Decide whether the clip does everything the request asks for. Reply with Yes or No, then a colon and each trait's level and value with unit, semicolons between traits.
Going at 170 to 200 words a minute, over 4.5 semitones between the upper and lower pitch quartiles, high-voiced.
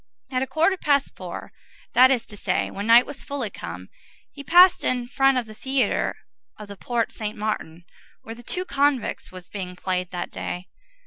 Yes: average, 190 wpm; average, 5.2 semitones; high, 235 Hz